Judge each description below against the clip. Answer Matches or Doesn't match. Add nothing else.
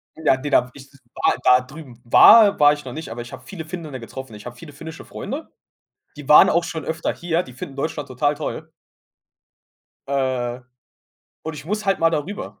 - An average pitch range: Matches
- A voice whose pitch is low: Doesn't match